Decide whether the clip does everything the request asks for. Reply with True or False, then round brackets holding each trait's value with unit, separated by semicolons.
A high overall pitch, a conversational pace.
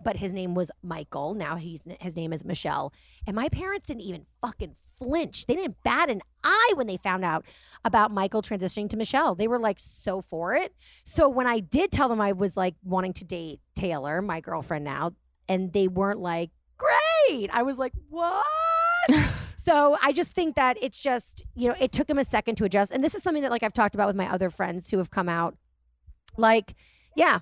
False (205 Hz; 215 wpm)